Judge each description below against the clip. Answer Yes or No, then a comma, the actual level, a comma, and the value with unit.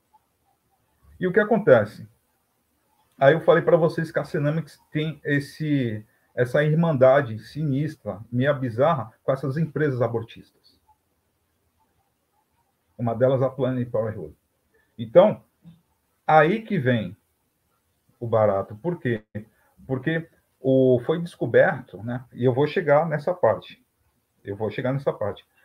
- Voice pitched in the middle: No, low, 130 Hz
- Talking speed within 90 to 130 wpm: Yes, average, 125 wpm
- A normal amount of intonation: No, wide, 5.7 semitones